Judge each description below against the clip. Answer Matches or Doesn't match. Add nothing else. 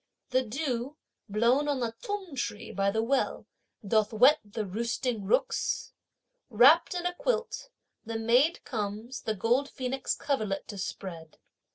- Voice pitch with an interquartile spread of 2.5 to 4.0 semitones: Doesn't match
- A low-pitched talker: Doesn't match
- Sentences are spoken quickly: Doesn't match